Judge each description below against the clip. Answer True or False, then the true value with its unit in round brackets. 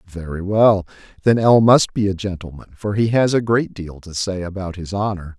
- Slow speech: False (200 wpm)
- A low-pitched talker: True (100 Hz)